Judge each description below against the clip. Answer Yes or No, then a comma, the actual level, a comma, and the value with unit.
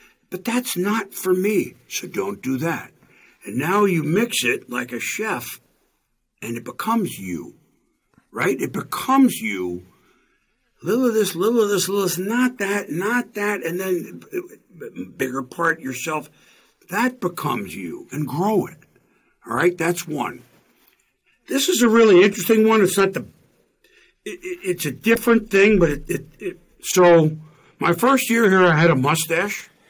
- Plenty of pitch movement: Yes, wide, 6.3 semitones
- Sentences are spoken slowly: No, average, 165 wpm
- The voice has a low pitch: No, medium, 185 Hz